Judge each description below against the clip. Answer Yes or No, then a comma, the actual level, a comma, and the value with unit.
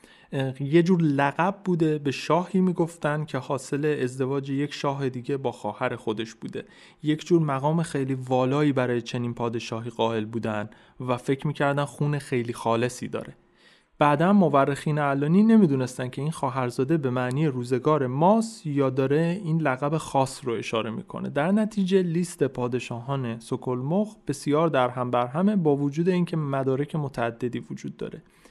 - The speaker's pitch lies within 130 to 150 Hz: Yes, medium, 140 Hz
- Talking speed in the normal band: Yes, average, 145 wpm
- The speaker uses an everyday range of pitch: Yes, average, 3.8 semitones